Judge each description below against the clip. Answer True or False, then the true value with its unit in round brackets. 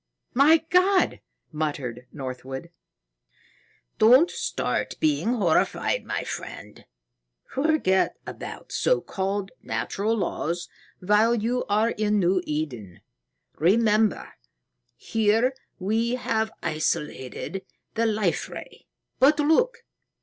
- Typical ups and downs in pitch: False (6.6 semitones)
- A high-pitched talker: True (215 Hz)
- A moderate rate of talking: False (95 wpm)